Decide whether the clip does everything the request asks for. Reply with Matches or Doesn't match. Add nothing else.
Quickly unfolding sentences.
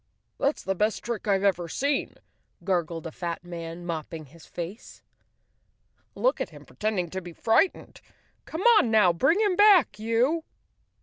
Doesn't match